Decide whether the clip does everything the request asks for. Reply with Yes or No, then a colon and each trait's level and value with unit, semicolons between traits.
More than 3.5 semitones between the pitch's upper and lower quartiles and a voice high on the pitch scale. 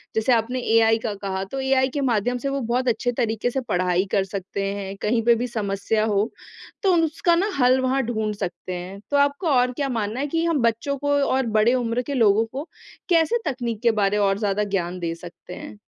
Yes: average, 4.7 semitones; high, 230 Hz